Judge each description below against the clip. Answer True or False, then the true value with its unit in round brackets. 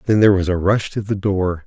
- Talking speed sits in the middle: False (290 wpm)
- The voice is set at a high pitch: False (100 Hz)